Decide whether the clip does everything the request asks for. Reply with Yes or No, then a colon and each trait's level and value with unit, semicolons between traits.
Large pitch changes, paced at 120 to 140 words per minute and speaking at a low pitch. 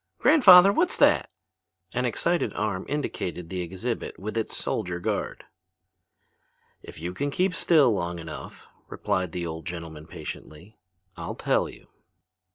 Yes: wide, 8.9 semitones; slow, 135 wpm; very low, 95 Hz